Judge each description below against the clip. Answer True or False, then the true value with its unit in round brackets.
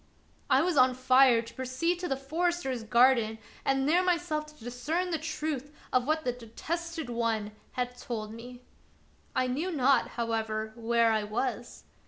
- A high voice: True (255 Hz)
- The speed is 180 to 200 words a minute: False (165 wpm)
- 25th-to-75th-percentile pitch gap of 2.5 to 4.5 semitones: False (4.9 semitones)